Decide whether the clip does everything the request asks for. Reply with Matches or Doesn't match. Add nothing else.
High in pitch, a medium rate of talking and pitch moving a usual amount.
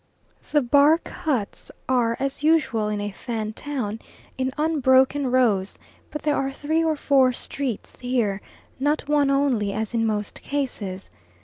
Matches